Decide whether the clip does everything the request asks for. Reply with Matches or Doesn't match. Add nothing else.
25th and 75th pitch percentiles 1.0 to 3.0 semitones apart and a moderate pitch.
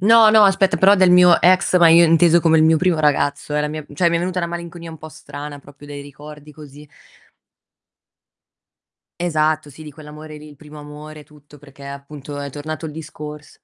Matches